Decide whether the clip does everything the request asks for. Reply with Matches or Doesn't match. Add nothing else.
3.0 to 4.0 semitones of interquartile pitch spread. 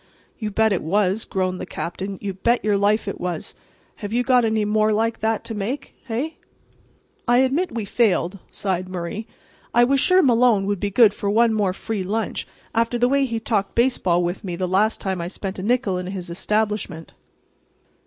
Matches